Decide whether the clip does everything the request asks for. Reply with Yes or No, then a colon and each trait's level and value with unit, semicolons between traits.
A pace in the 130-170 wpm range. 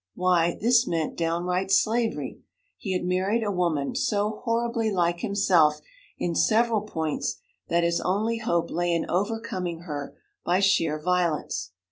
Yes: average, 140 wpm